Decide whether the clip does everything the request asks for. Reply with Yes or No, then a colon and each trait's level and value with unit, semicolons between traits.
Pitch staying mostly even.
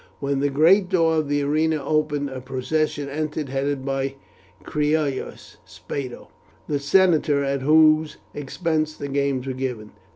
Yes: narrow, 2.2 semitones